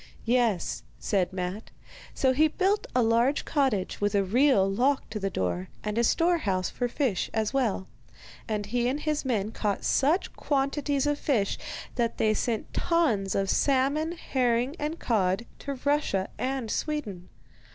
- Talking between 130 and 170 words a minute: Yes, average, 160 wpm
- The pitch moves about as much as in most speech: No, wide, 5.8 semitones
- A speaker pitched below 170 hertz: No, high, 240 Hz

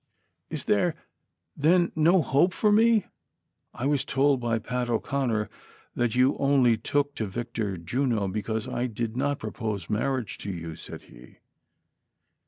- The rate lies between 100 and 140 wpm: No, average, 155 wpm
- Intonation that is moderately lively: Yes, average, 4.6 semitones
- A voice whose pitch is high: No, low, 120 Hz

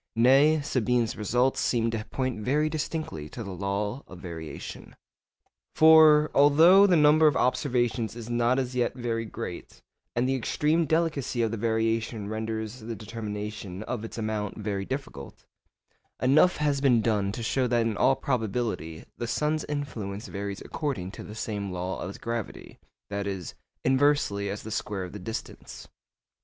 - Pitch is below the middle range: Yes, low, 115 Hz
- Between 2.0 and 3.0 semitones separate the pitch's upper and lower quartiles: No, average, 4.7 semitones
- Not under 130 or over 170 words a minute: Yes, average, 155 wpm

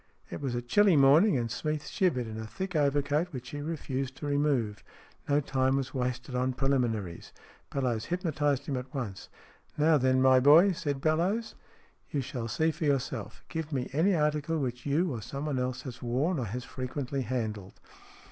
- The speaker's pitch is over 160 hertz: No, low, 135 Hz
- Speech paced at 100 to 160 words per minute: No, average, 185 wpm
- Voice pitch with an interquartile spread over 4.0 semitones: No, average, 3.3 semitones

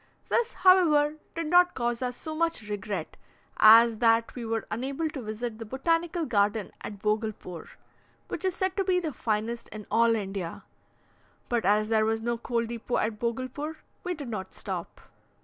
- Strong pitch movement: Yes, wide, 6.2 semitones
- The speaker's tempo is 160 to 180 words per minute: Yes, average, 170 wpm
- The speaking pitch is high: Yes, high, 235 Hz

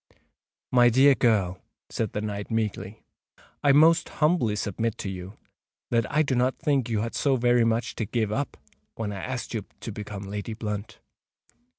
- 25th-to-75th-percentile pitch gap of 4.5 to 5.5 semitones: No, average, 3.5 semitones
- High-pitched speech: No, low, 115 Hz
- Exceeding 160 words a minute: Yes, average, 175 wpm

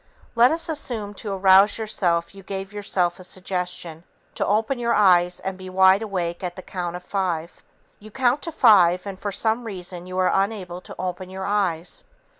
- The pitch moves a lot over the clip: No, narrow, 2.6 semitones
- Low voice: No, high, 190 Hz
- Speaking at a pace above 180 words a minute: Yes, average, 190 wpm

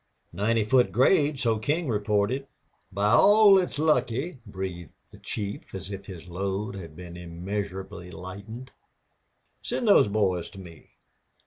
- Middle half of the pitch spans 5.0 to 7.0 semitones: Yes, wide, 5.5 semitones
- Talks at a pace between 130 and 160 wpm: Yes, slow, 135 wpm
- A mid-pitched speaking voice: No, low, 105 Hz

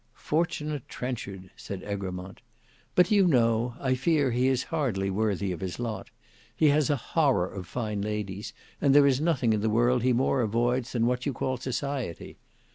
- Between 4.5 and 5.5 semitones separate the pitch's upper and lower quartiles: Yes, average, 4.9 semitones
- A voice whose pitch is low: Yes, low, 120 Hz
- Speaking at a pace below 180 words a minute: No, average, 185 wpm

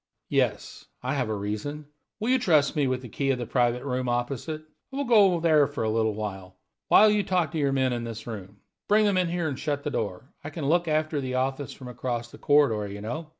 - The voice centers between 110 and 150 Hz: Yes, low, 135 Hz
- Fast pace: Yes, fast, 240 wpm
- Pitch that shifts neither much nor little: Yes, average, 5.0 semitones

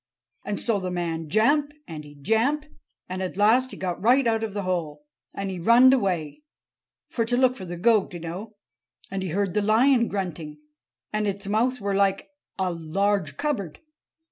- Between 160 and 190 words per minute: Yes, average, 180 wpm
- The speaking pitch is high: Yes, high, 200 Hz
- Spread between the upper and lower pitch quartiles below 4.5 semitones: No, average, 4.8 semitones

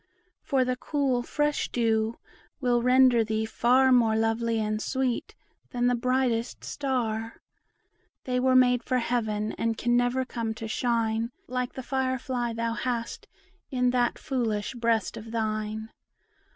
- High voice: Yes, high, 240 Hz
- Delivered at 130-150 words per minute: Yes, average, 145 wpm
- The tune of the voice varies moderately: No, narrow, 2.1 semitones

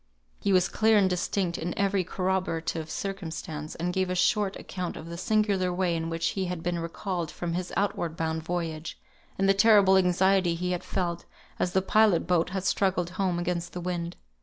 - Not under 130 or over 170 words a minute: No, average, 190 wpm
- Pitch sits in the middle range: Yes, medium, 180 Hz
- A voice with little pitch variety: Yes, narrow, 2.1 semitones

